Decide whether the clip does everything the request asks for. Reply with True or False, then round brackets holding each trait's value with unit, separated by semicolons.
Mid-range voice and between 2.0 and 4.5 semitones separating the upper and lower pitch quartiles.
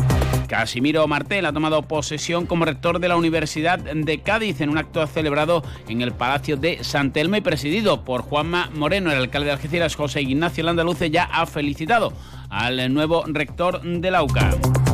True (155 Hz; 3.0 semitones)